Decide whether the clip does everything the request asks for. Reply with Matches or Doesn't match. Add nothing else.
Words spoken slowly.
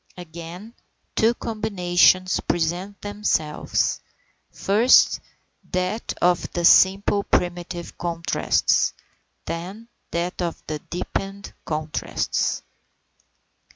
Matches